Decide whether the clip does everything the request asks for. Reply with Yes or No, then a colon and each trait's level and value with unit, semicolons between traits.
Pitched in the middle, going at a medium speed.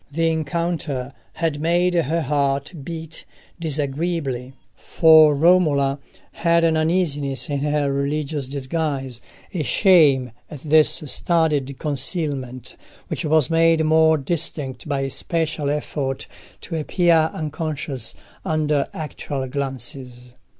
No: medium, 150 Hz; slow, 110 wpm